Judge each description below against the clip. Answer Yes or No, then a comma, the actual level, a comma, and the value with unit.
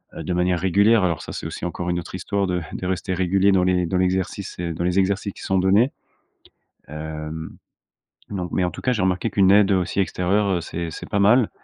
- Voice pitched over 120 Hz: No, very low, 95 Hz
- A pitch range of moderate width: No, narrow, 2.0 semitones